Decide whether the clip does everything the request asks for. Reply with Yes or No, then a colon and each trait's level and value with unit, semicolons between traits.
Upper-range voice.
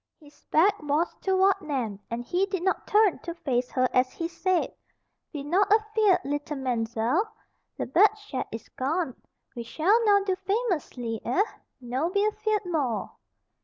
Yes: very high, 335 Hz